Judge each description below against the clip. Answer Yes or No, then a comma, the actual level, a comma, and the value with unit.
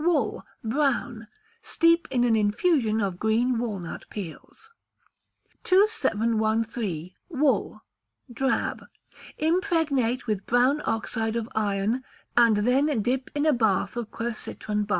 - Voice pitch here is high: Yes, high, 235 Hz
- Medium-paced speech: No, slow, 110 wpm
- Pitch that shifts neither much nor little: Yes, average, 4.1 semitones